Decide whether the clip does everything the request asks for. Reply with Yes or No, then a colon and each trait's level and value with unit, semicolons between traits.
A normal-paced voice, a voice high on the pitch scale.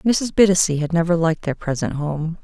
No: average, 195 wpm; medium, 170 Hz